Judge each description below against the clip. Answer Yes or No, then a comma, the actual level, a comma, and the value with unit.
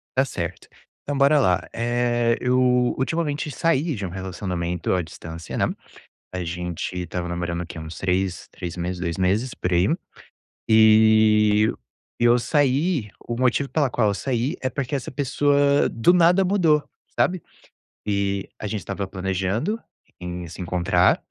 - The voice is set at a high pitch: No, low, 105 Hz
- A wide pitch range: Yes, wide, 7.1 semitones